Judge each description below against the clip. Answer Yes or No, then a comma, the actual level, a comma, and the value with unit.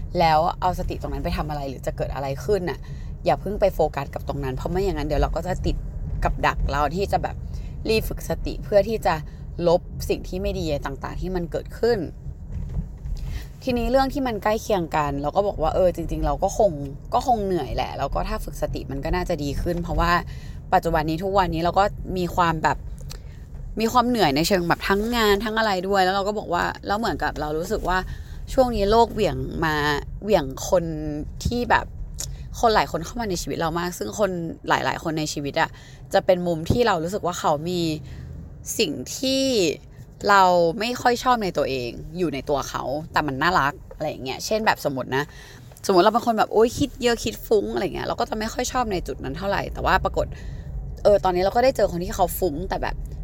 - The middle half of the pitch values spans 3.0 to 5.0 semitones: No, wide, 5.6 semitones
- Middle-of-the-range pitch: Yes, medium, 175 Hz